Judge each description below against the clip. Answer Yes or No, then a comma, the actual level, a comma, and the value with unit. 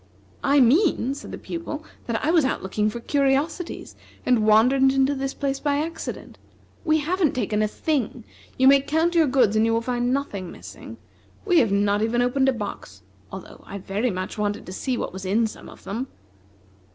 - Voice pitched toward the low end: No, very high, 255 Hz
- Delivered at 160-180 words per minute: No, average, 195 wpm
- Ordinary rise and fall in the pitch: Yes, average, 5.0 semitones